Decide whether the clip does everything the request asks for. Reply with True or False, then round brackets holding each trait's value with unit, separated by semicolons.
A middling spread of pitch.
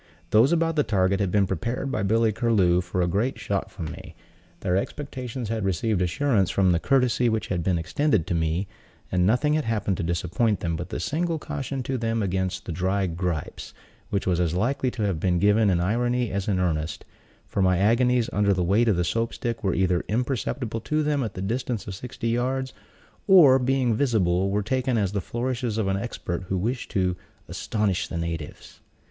True (5.0 semitones)